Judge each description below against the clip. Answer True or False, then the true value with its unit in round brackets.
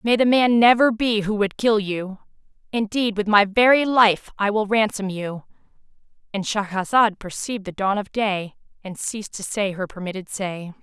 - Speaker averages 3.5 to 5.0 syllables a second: True (4.8 syllables/s)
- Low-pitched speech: False (205 Hz)